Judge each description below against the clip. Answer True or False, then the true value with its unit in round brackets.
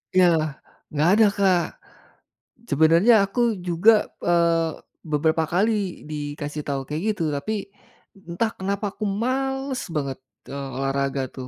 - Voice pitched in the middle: True (165 Hz)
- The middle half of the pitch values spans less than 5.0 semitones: False (5.5 semitones)